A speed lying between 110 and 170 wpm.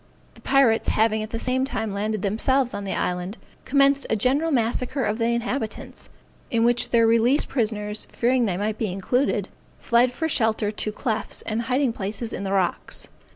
No: average, 180 wpm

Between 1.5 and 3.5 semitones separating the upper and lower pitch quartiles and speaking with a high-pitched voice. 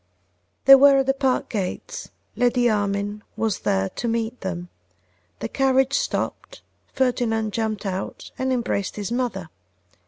No: average, 4.6 semitones; high, 230 Hz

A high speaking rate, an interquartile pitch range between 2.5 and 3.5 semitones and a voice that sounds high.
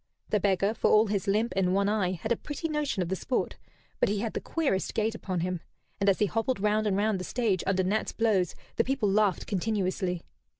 Yes: fast, 225 wpm; average, 2.9 semitones; high, 205 Hz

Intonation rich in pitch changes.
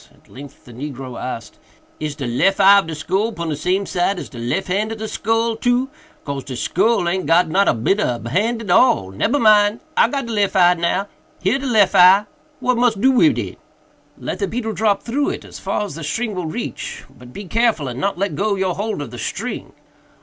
Yes: wide, 6.3 semitones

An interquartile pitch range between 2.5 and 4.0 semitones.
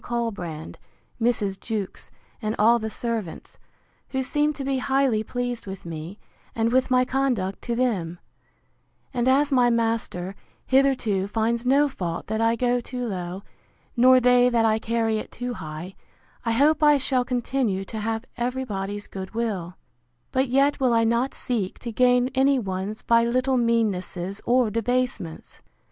Yes: average, 3.7 semitones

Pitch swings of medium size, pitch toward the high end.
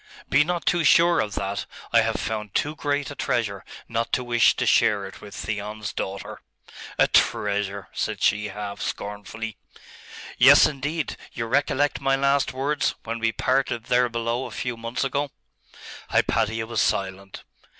No: average, 4.8 semitones; low, 115 Hz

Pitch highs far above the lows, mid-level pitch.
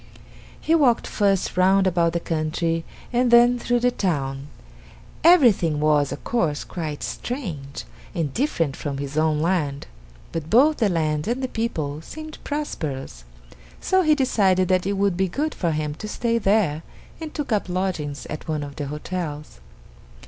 Yes: wide, 7.6 semitones; medium, 180 Hz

